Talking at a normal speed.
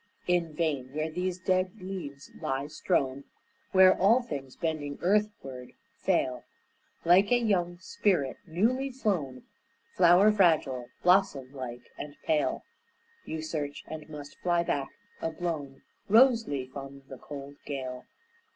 No: slow, 130 wpm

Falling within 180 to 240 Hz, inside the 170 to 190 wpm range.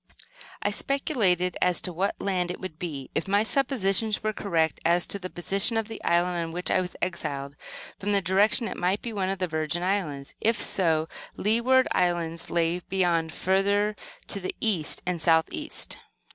Yes: medium, 185 Hz; average, 185 wpm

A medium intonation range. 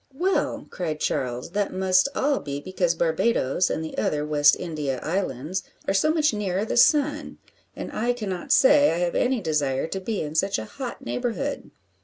No: wide, 7.7 semitones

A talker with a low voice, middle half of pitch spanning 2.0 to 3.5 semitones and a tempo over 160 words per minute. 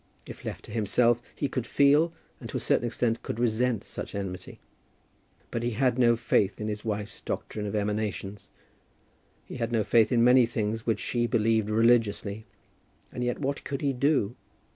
Yes: low, 115 Hz; narrow, 2.6 semitones; average, 180 wpm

